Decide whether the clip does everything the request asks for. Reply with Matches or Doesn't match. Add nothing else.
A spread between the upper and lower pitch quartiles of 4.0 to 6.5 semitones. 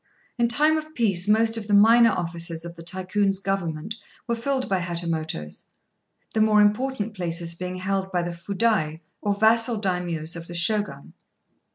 Matches